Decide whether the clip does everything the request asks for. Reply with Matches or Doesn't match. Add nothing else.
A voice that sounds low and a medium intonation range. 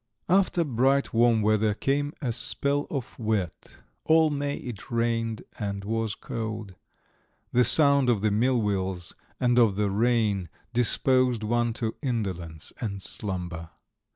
Matches